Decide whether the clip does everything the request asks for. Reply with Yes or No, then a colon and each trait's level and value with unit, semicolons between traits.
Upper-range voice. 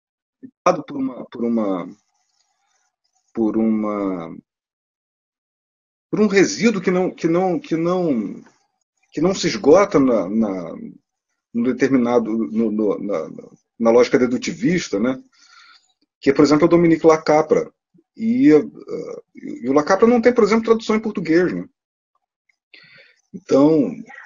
Yes: high, 215 Hz